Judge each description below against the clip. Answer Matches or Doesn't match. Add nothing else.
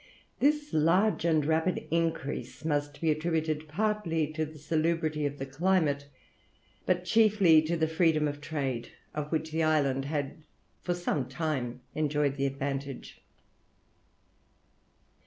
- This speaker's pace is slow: Matches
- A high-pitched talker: Doesn't match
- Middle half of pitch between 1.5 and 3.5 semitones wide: Matches